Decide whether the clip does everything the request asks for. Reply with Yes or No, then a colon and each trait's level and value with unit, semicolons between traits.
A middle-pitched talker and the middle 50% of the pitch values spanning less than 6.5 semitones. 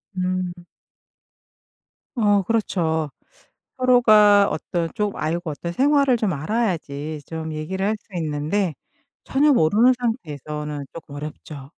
Yes: medium, 180 Hz; wide, 5.9 semitones